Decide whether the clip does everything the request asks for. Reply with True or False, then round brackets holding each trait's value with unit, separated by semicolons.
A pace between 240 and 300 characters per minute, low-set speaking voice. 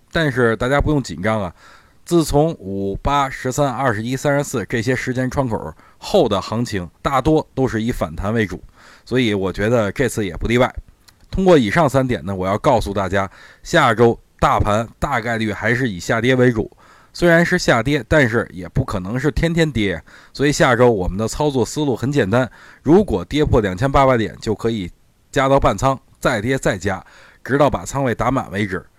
True (280 characters per minute; 120 Hz)